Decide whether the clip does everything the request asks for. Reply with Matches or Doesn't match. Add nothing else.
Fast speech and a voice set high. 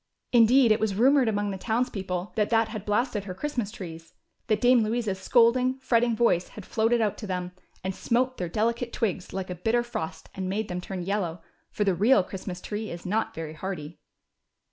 Doesn't match